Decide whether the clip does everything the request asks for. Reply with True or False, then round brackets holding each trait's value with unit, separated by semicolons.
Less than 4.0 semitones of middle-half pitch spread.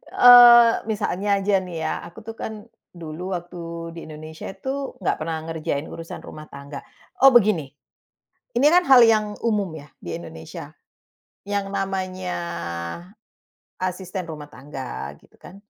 False (5.4 semitones)